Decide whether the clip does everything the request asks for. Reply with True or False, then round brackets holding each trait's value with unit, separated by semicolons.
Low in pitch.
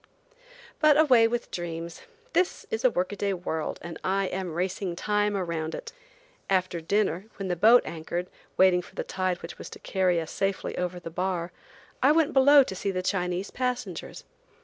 False (185 Hz)